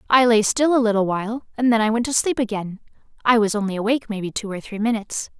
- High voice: Yes, high, 225 Hz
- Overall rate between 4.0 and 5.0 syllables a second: No, 6.8 syllables/s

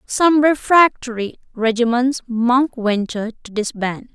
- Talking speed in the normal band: No, slow, 100 wpm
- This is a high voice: Yes, high, 245 Hz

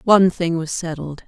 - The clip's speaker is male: No, female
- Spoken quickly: No, average, 190 wpm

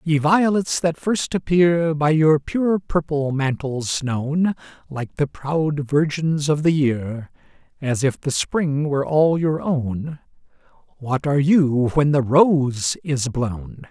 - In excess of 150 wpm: No, average, 145 wpm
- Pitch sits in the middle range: Yes, medium, 150 Hz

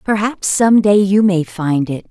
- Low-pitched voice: No, high, 190 Hz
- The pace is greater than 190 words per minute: Yes, average, 200 wpm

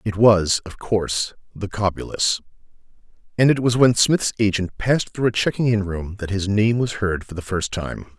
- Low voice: Yes, low, 105 Hz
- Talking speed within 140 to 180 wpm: No, average, 200 wpm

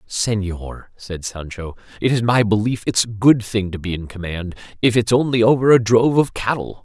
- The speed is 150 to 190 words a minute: No, average, 200 wpm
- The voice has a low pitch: Yes, low, 110 Hz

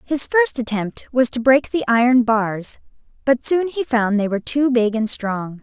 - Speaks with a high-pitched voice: Yes, high, 245 Hz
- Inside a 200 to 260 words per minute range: Yes, fast, 205 wpm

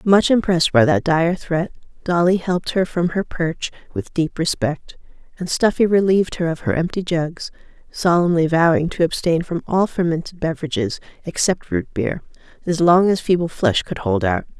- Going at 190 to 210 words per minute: No, average, 175 wpm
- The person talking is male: No, female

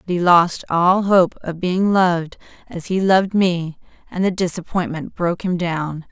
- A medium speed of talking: Yes, average, 175 wpm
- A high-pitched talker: No, medium, 175 Hz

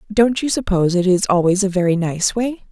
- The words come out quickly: Yes, fast, 220 wpm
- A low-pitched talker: No, high, 195 Hz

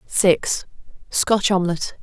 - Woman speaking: Yes, female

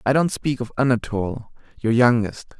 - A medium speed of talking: Yes, average, 160 wpm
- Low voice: Yes, low, 120 Hz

